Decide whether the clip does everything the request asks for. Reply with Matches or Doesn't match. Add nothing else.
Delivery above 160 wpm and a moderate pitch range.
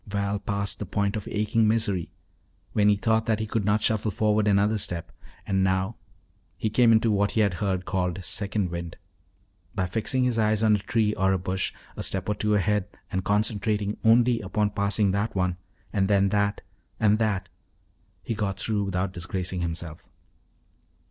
Doesn't match